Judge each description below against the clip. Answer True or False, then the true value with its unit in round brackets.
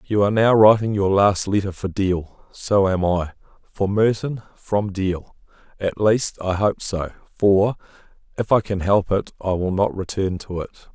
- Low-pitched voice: True (100 Hz)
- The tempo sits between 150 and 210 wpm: True (180 wpm)